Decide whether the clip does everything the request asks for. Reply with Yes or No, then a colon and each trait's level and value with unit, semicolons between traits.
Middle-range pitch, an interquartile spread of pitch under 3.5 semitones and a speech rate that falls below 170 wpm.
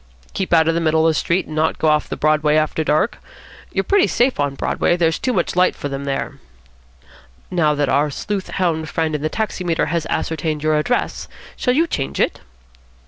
No: medium, 160 Hz; average, 2.9 semitones; fast, 205 wpm